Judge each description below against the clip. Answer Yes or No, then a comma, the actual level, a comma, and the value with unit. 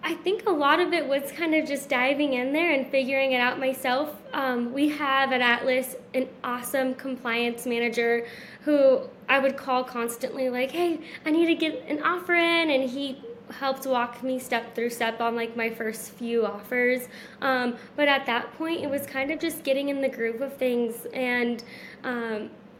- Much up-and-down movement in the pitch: No, average, 2.8 semitones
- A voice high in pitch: Yes, very high, 260 Hz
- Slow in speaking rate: No, average, 190 wpm